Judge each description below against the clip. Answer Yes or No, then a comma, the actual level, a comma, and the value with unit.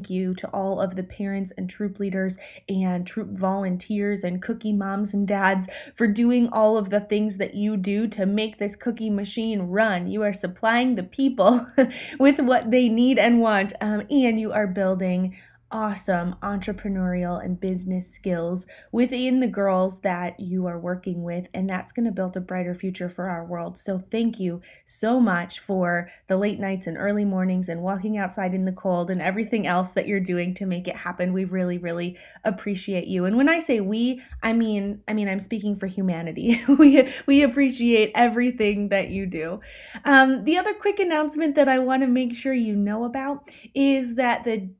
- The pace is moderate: Yes, average, 195 wpm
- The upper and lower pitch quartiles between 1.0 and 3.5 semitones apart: No, average, 4.0 semitones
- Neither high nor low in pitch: No, high, 205 Hz